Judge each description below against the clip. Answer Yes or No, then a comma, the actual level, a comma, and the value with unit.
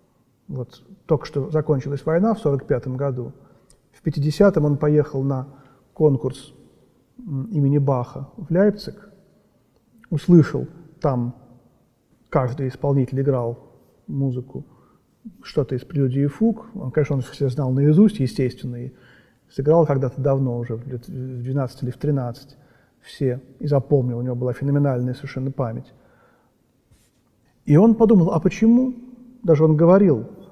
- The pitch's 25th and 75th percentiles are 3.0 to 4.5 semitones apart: Yes, average, 3.7 semitones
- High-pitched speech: No, medium, 140 Hz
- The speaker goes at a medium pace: Yes, average, 125 wpm